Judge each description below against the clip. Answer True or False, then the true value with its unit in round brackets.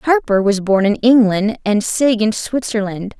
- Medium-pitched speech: False (220 Hz)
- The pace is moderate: True (170 wpm)